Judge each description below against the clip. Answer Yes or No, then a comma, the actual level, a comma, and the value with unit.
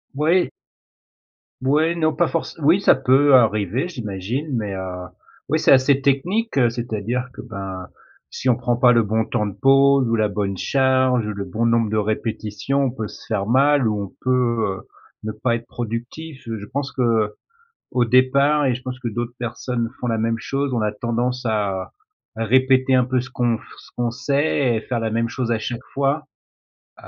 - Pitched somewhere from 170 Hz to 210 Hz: No, low, 120 Hz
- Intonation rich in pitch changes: No, average, 3.4 semitones